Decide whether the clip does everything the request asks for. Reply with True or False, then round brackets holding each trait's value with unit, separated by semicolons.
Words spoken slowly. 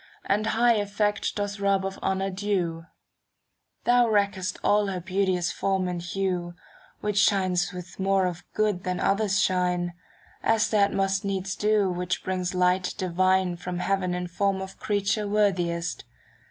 False (155 wpm)